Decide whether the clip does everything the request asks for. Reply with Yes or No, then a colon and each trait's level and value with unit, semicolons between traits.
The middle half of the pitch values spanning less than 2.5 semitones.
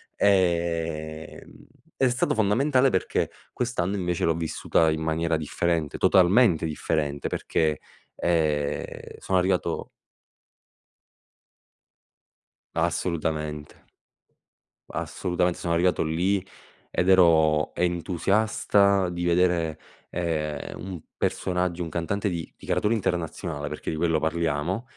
No: average, 2.9 semitones